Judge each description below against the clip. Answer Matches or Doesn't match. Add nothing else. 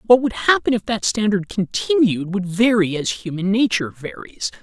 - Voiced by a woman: Doesn't match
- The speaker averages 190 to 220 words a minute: Doesn't match